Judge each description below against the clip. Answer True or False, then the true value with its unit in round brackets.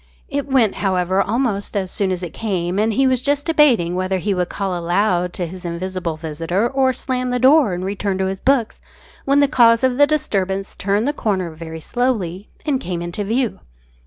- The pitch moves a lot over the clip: True (5.8 semitones)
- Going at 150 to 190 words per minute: False (200 wpm)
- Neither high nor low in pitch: False (200 Hz)